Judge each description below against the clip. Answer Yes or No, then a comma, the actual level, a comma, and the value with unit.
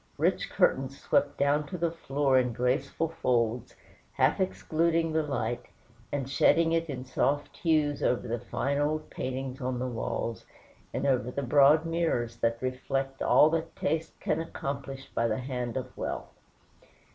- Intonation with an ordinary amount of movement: Yes, average, 3.7 semitones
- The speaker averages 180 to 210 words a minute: No, average, 160 wpm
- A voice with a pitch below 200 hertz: Yes, low, 135 Hz